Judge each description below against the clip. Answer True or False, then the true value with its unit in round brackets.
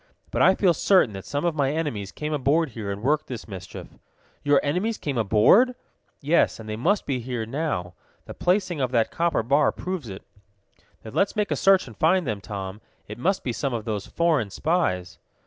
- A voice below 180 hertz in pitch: True (140 Hz)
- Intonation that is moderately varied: False (7.6 semitones)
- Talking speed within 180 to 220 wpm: True (200 wpm)